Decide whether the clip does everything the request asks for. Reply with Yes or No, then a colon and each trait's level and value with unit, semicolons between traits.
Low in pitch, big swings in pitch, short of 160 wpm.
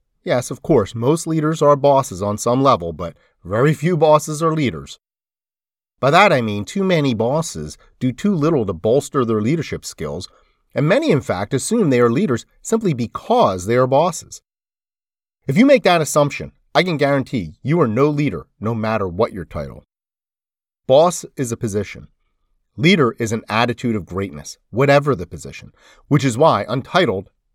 No: low, 125 Hz; wide, 6.5 semitones; average, 170 wpm